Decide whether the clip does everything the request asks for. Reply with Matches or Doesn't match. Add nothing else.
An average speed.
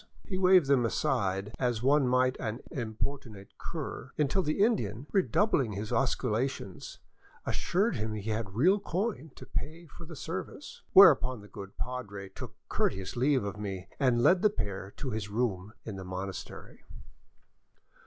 Matches